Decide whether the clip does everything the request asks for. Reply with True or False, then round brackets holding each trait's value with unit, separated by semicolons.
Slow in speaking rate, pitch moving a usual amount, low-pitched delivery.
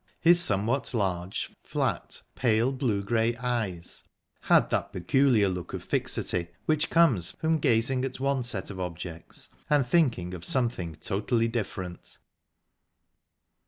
False (125 wpm; 6.0 semitones; 115 Hz)